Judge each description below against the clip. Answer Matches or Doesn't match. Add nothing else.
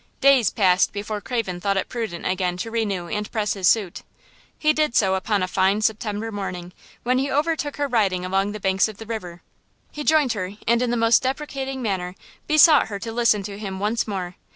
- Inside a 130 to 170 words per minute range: Doesn't match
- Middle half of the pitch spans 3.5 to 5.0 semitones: Matches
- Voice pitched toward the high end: Matches